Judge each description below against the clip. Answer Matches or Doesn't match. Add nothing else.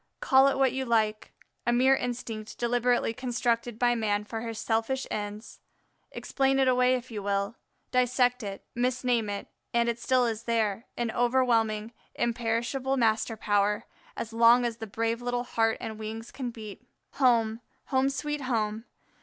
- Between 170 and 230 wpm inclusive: Doesn't match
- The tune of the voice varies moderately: Doesn't match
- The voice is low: Doesn't match